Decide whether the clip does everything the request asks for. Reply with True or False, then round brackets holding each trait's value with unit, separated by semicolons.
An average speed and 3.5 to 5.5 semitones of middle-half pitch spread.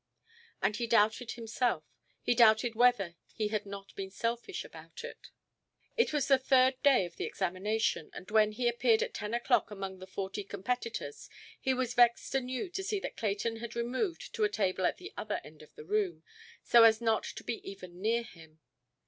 True (190 wpm; 3.9 semitones)